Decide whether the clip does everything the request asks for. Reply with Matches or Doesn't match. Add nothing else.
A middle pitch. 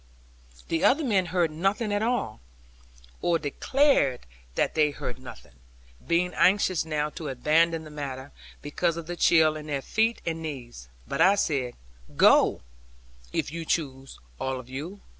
Matches